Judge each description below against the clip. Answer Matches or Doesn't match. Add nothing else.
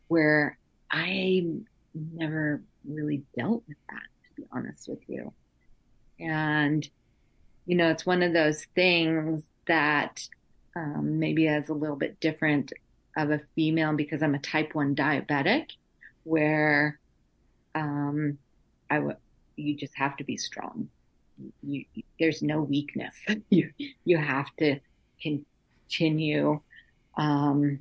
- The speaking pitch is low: Doesn't match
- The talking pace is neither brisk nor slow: Doesn't match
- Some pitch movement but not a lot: Doesn't match